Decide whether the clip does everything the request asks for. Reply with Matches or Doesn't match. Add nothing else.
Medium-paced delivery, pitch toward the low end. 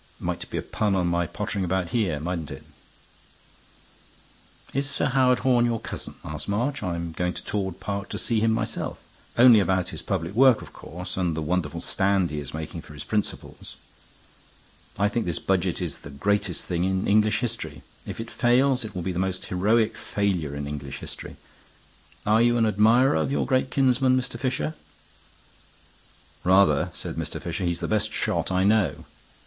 Matches